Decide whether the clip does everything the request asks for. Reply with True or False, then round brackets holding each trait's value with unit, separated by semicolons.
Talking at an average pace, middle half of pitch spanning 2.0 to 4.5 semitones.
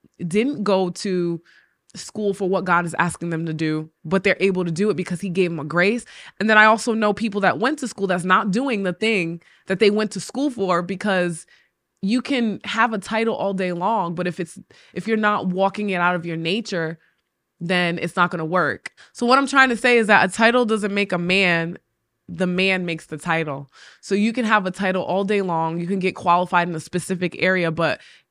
False (230 wpm; 3.4 semitones)